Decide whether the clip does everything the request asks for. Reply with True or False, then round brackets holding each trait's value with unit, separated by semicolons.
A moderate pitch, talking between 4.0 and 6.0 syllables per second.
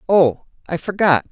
True (175 Hz; 4.4 syllables/s)